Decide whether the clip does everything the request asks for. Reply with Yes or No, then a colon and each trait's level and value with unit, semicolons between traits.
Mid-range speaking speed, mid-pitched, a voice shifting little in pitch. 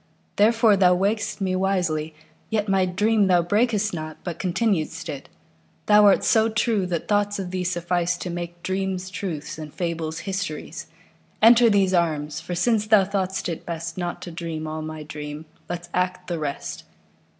No: average, 150 wpm; medium, 180 Hz; average, 3.4 semitones